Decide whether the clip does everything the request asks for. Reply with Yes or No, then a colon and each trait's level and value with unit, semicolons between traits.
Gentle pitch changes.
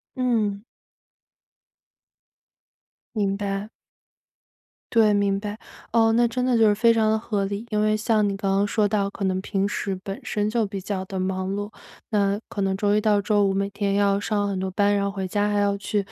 Yes: narrow, 1.4 semitones